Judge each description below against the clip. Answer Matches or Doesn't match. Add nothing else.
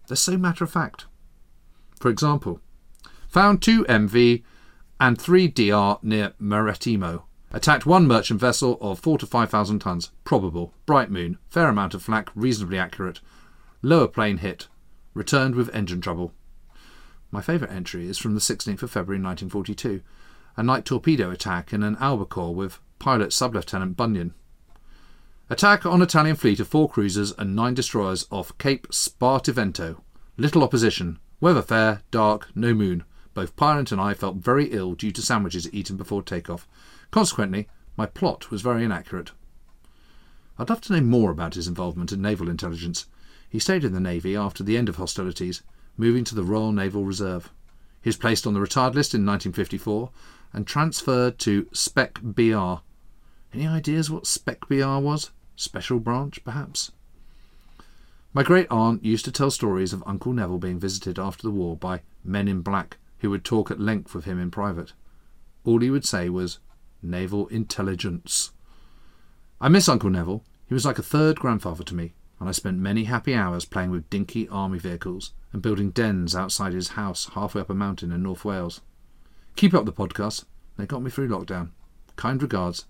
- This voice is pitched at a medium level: Doesn't match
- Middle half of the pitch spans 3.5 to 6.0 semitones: Matches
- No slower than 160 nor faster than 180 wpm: Matches